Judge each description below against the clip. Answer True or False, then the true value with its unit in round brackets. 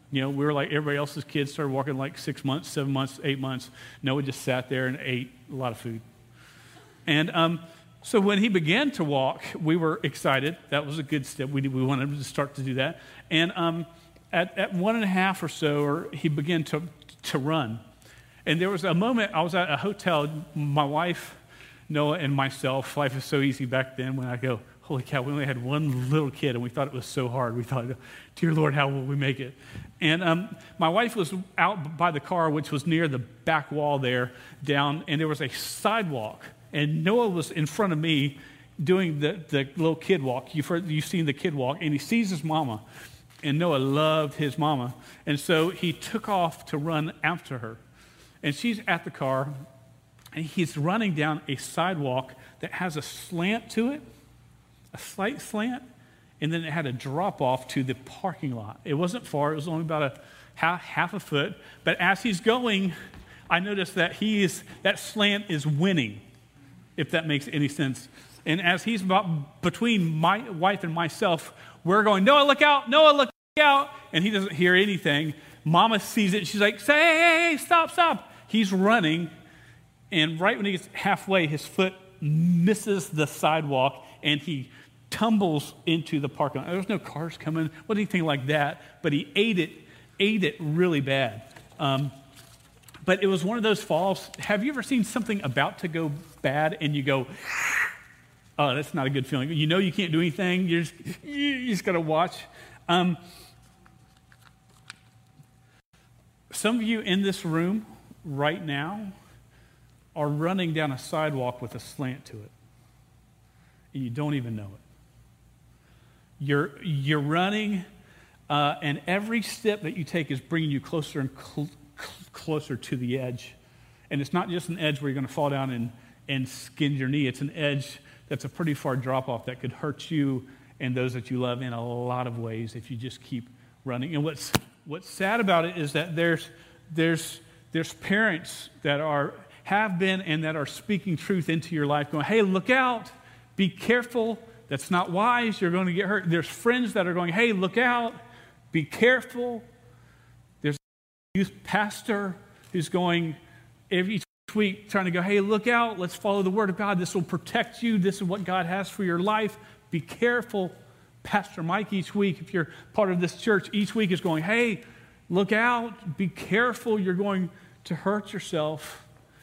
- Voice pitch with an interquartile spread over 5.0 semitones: True (5.5 semitones)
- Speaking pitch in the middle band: True (155 Hz)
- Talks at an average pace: True (190 wpm)